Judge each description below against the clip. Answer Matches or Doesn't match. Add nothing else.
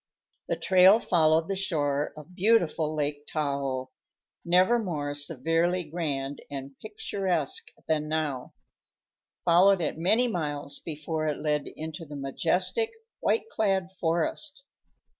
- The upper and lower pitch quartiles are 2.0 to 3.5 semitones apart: Doesn't match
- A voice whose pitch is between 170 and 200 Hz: Doesn't match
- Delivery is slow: Matches